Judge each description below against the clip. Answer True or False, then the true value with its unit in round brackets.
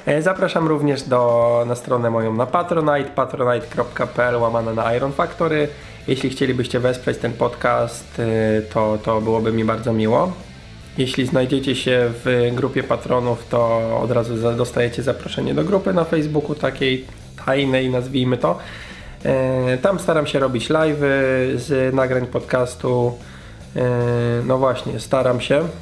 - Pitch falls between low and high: False (125 Hz)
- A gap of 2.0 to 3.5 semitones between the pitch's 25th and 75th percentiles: True (2.5 semitones)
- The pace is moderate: True (130 wpm)